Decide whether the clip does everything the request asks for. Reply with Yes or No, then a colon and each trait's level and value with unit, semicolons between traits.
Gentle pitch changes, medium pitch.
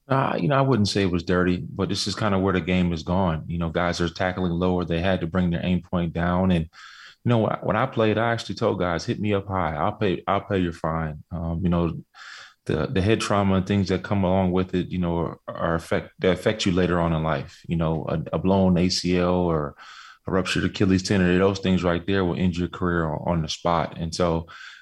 No: narrow, 2.3 semitones; very low, 90 Hz